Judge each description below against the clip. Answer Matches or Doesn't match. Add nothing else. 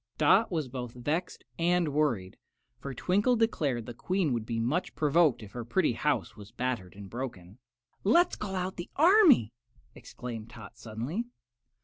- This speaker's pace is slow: Doesn't match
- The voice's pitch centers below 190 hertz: Matches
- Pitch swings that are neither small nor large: Doesn't match